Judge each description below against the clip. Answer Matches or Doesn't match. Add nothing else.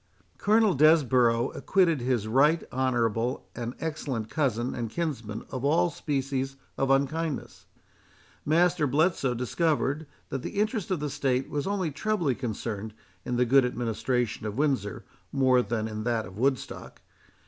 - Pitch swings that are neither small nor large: Matches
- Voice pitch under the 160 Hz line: Matches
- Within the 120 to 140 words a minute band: Matches